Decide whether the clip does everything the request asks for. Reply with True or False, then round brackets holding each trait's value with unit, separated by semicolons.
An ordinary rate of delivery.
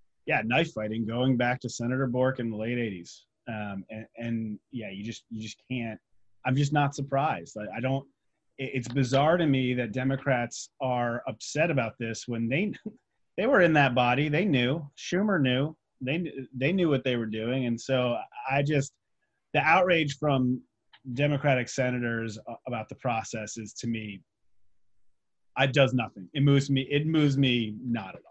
True (180 wpm)